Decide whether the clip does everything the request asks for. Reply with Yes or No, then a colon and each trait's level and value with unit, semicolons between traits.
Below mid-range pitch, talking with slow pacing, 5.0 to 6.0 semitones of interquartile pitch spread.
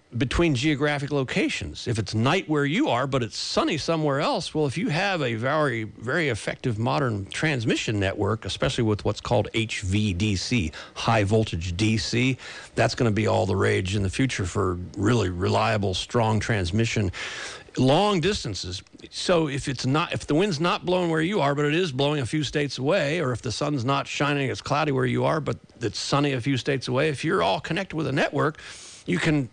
No: low, 130 Hz; average, 195 wpm; wide, 5.5 semitones